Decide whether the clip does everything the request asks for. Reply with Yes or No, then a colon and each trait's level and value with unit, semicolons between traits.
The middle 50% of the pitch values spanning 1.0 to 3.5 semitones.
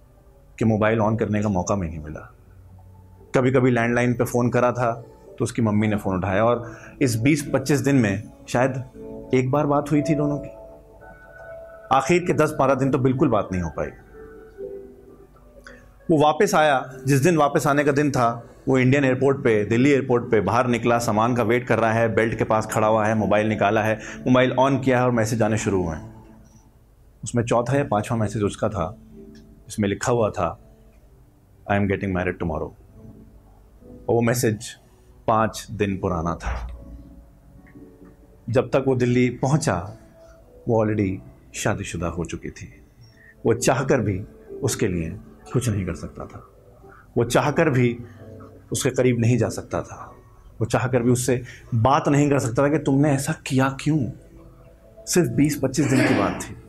No: average, 4.1 semitones